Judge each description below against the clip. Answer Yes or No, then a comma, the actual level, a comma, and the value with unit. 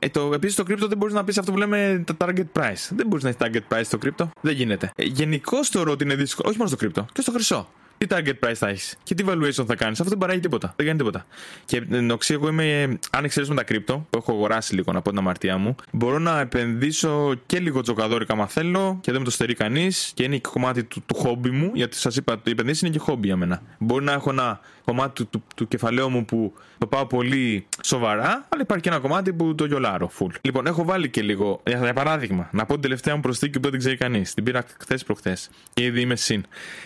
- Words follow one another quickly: Yes, fast, 250 wpm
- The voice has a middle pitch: No, low, 130 Hz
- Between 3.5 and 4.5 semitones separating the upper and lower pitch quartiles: No, average, 5.3 semitones